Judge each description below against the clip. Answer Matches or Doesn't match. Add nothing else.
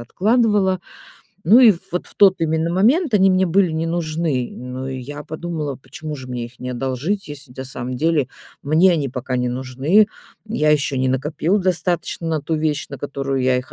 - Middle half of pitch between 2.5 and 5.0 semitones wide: Doesn't match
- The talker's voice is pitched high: Doesn't match